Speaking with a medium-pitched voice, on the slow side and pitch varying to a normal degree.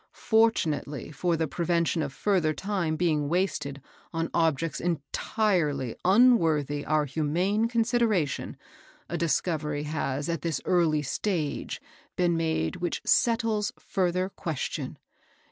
Yes: medium, 165 Hz; slow, 110 wpm; average, 4.0 semitones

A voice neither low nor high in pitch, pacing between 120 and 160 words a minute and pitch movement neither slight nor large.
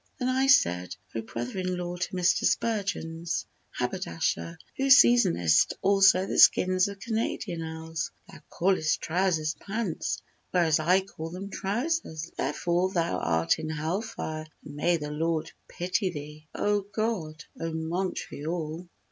Yes: medium, 175 Hz; average, 140 wpm; average, 3.8 semitones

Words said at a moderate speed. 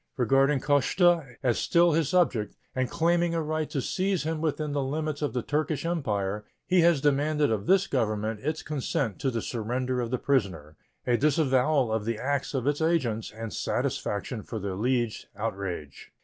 Yes: average, 175 wpm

